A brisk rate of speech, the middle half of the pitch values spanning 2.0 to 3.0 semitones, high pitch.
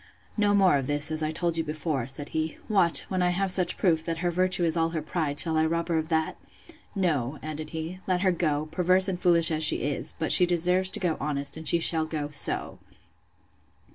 No: fast, 225 wpm; narrow, 2.5 semitones; medium, 165 Hz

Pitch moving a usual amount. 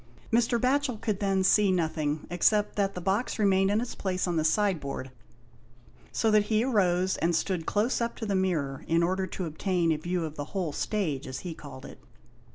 Yes: average, 4.4 semitones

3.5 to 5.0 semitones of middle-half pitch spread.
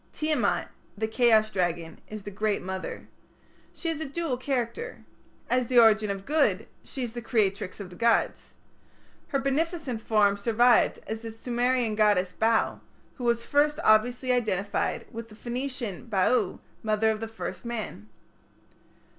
No: average, 3.0 semitones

